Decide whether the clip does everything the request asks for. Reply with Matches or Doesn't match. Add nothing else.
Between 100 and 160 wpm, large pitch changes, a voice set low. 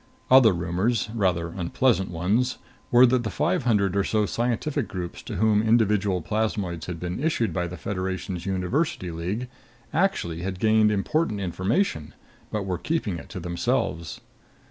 Doesn't match